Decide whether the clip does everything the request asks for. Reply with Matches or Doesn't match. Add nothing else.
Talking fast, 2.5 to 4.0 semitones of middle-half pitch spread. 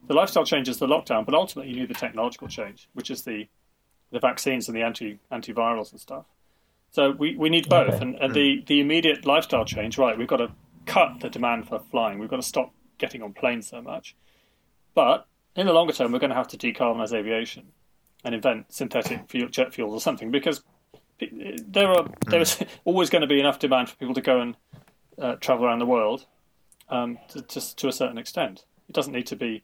Doesn't match